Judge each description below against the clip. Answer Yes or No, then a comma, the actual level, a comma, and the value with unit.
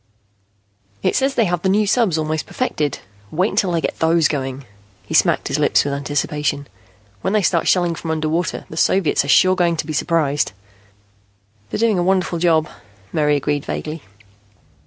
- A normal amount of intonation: Yes, average, 3.7 semitones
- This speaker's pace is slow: No, average, 175 wpm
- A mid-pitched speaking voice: Yes, medium, 165 Hz